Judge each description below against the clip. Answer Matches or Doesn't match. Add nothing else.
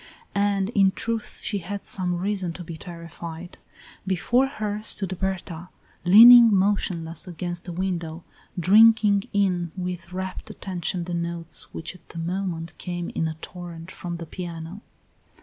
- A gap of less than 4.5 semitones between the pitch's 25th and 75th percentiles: Matches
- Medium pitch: Matches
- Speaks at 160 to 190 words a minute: Doesn't match